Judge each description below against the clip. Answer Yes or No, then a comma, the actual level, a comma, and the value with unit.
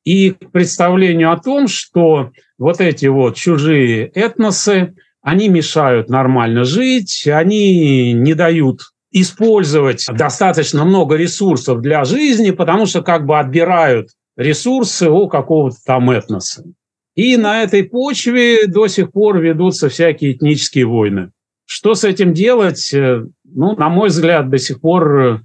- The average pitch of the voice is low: No, medium, 165 Hz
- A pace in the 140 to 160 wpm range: No, average, 130 wpm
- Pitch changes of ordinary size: No, wide, 6.1 semitones